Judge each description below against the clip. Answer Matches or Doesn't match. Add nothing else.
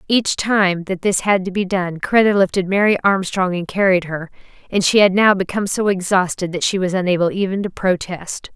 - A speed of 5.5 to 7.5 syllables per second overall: Doesn't match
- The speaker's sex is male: Doesn't match